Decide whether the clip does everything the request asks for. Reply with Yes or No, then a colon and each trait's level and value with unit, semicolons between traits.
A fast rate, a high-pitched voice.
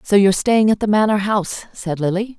Yes: fast, 225 wpm; high, 205 Hz